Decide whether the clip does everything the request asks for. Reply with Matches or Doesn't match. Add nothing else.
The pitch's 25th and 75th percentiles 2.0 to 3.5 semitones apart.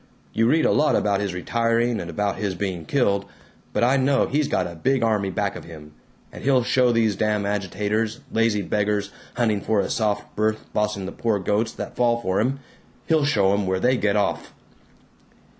Matches